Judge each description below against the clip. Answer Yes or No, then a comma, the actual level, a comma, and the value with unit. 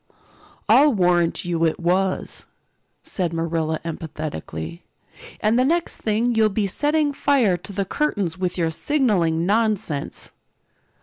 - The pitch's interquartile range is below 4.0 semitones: No, wide, 5.5 semitones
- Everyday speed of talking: No, slow, 125 wpm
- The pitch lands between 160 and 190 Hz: Yes, medium, 185 Hz